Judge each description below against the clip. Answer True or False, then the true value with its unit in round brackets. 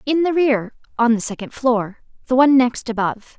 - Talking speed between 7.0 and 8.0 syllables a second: False (5.4 syllables/s)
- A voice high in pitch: True (245 Hz)